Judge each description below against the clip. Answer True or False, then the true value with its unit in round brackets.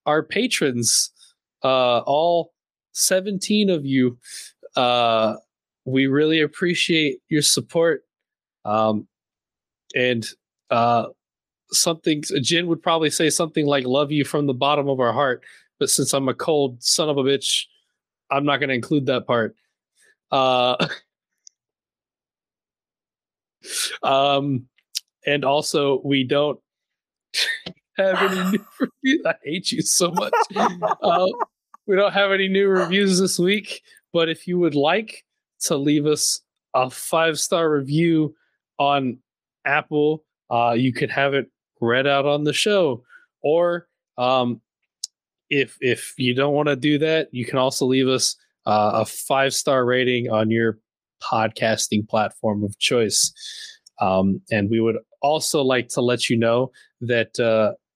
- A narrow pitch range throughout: False (4.8 semitones)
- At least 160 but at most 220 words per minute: False (140 wpm)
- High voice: False (140 Hz)